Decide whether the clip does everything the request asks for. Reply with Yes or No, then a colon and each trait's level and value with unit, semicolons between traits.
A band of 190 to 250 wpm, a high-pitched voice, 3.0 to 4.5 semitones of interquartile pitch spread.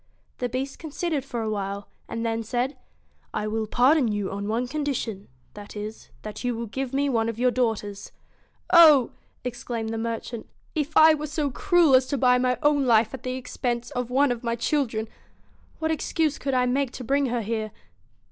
Yes: fast, 205 wpm; high, 245 Hz; average, 3.8 semitones